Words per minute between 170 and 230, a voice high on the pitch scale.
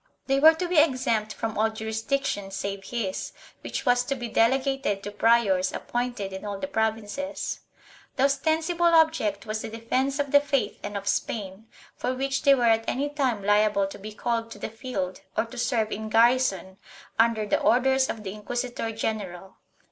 Yes: average, 185 wpm; high, 230 Hz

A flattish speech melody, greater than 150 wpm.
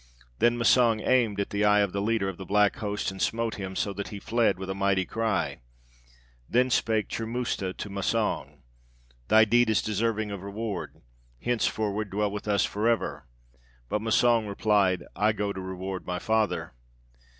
Yes: narrow, 2.3 semitones; average, 175 wpm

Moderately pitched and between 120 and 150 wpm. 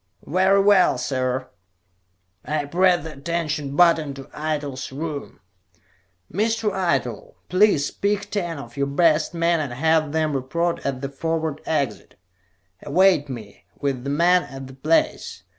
Yes: medium, 155 Hz; average, 140 wpm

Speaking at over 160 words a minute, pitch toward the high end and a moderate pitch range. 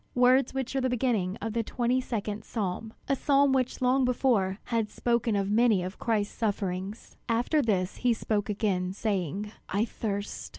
Yes: average, 170 wpm; high, 225 Hz; average, 3.7 semitones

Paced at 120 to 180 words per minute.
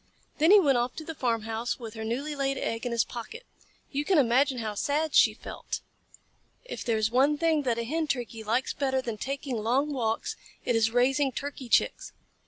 No: average, 200 wpm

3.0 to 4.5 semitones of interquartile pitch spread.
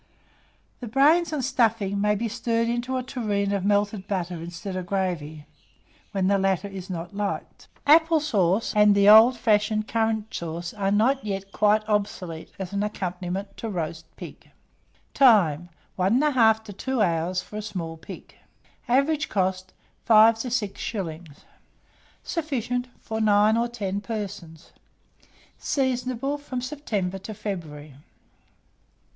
Yes: average, 4.0 semitones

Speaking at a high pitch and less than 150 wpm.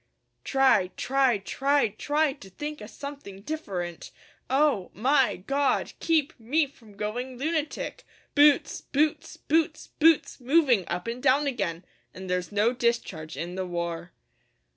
Yes: very high, 255 Hz; slow, 135 wpm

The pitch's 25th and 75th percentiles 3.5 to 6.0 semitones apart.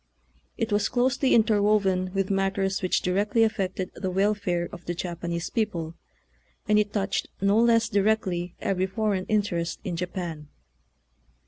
No: average, 2.7 semitones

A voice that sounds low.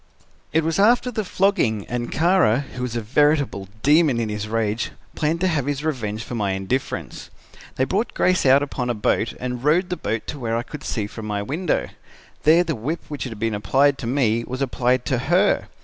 Yes: low, 130 Hz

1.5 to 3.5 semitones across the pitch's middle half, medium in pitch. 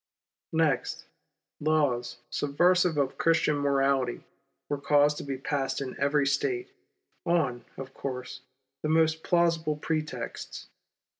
Yes: average, 2.8 semitones; medium, 145 Hz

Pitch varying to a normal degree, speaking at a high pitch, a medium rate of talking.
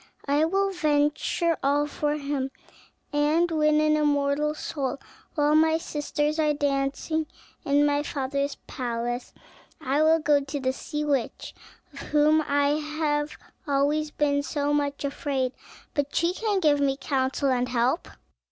No: narrow, 1.6 semitones; very high, 290 Hz; average, 145 wpm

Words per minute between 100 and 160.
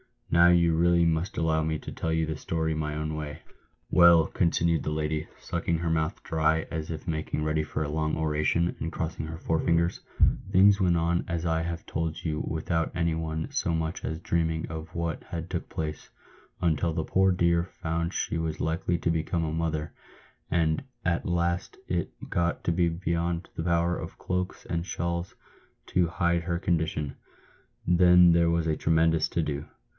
No: average, 185 wpm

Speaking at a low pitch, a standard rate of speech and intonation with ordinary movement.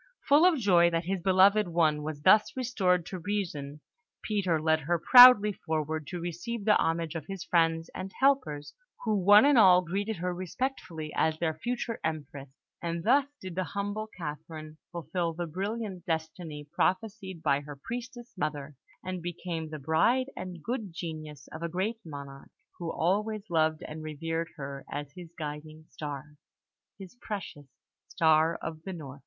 No: medium, 170 Hz; average, 160 wpm; average, 4.3 semitones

